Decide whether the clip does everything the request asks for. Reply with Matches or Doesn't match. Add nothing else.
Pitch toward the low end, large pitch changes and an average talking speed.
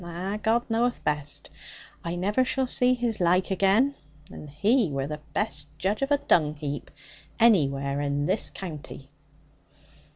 Doesn't match